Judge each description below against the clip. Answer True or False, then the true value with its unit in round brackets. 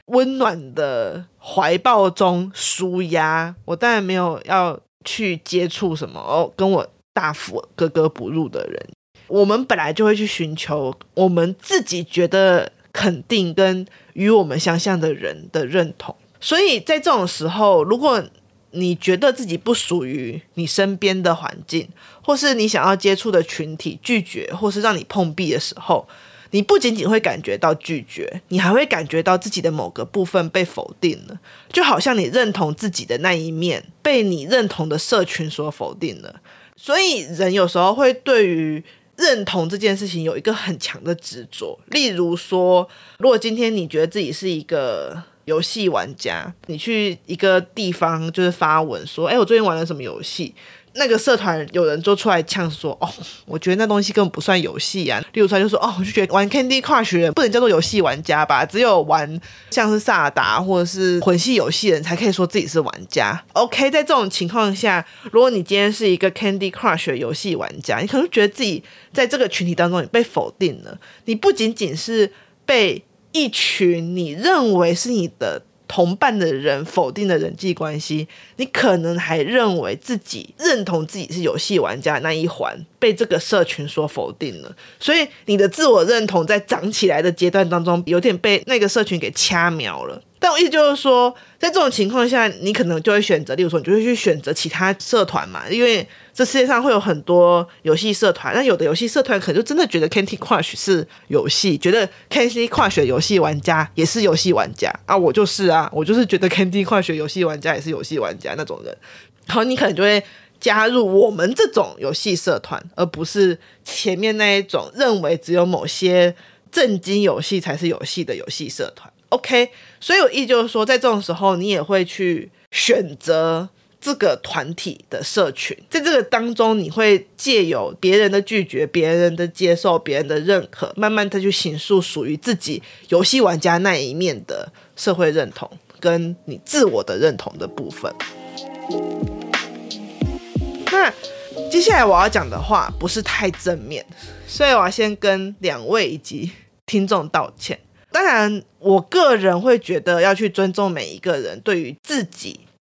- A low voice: False (190 Hz)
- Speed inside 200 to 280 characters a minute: False (290 characters per minute)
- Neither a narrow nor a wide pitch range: True (4.5 semitones)